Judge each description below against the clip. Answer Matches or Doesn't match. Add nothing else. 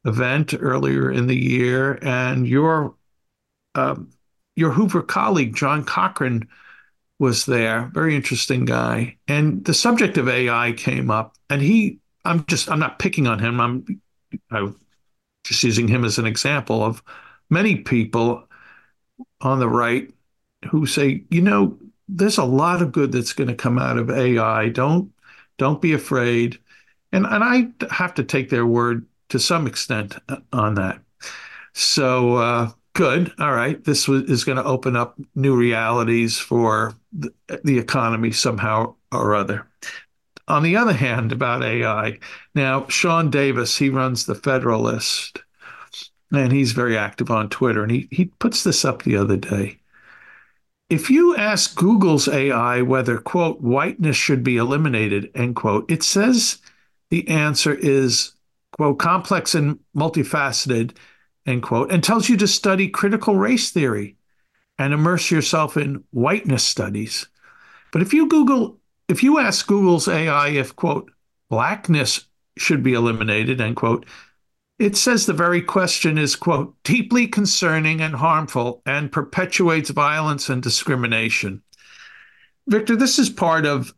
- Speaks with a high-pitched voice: Doesn't match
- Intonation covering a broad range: Matches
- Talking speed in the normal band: Matches